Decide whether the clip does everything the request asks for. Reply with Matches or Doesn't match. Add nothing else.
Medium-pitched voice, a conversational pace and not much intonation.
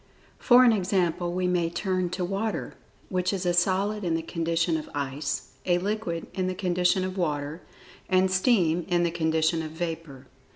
Matches